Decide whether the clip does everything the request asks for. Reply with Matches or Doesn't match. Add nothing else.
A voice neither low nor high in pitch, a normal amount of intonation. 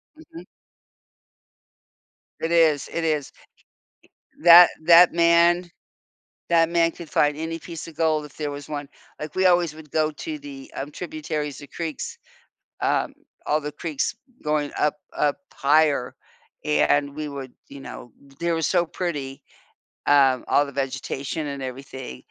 Matches